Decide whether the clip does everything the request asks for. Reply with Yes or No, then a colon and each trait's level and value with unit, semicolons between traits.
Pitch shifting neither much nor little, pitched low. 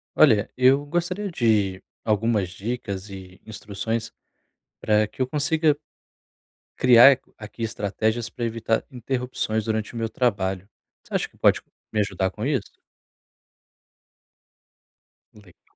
Yes: average, 3.6 semitones; low, 110 Hz